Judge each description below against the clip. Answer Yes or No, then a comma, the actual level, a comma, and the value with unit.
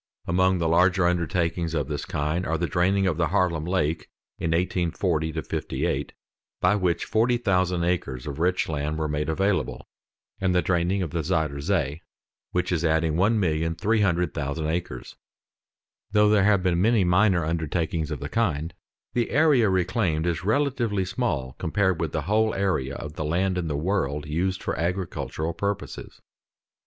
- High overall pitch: No, very low, 85 Hz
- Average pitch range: Yes, average, 3.2 semitones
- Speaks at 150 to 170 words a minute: Yes, average, 155 wpm